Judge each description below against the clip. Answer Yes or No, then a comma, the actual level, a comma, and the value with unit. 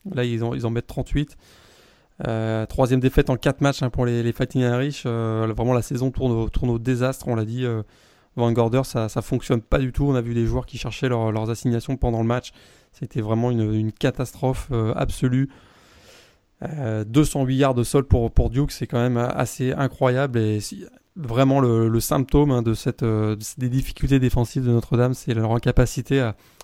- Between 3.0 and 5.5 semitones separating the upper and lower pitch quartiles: No, narrow, 2.4 semitones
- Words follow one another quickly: No, average, 205 wpm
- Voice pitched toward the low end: Yes, low, 125 Hz